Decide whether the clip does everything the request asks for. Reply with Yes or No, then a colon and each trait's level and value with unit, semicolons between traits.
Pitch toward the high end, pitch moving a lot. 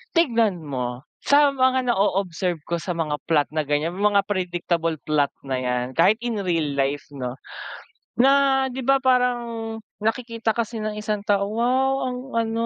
Yes: high, 205 Hz; wide, 7.1 semitones